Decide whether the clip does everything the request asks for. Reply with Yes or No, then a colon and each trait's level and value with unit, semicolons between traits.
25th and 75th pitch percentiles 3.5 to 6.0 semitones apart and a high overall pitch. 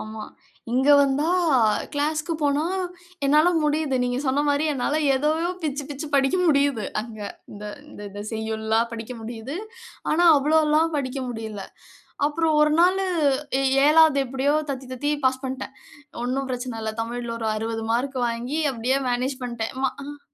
Yes: average, 4.3 semitones; very high, 265 Hz